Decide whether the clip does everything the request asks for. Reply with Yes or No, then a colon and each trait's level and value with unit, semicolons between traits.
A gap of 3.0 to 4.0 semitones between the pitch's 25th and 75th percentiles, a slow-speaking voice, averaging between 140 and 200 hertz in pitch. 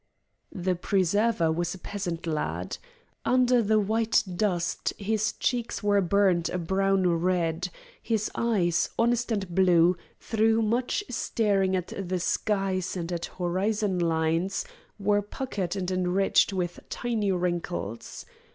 Yes: average, 3.4 semitones; slow, 125 wpm; high, 190 Hz